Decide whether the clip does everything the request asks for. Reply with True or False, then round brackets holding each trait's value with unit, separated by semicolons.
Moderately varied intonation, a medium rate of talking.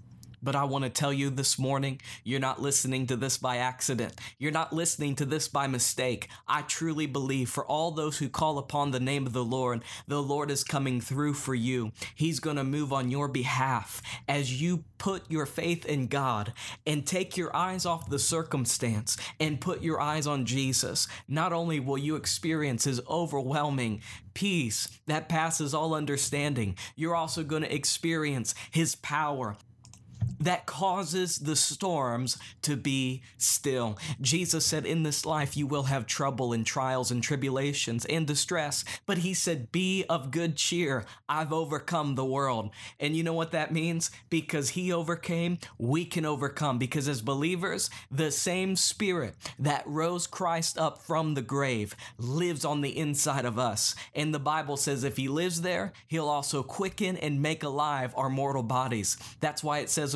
True (3.7 semitones; 175 wpm)